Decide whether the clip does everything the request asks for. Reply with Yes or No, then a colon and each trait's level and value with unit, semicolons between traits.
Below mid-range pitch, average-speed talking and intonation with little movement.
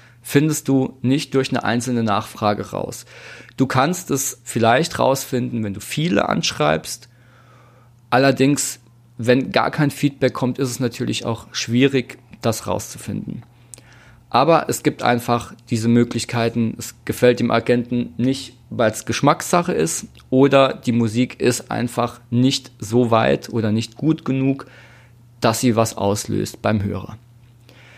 Yes: low, 120 Hz; average, 135 wpm; narrow, 2.1 semitones